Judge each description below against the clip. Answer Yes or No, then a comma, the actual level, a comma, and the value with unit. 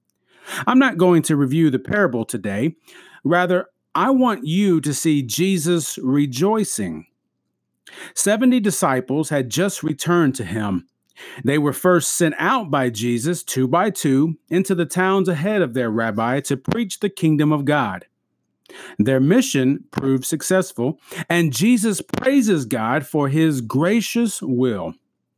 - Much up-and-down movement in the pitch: Yes, wide, 6.3 semitones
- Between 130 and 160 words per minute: Yes, slow, 135 wpm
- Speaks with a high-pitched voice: No, medium, 160 Hz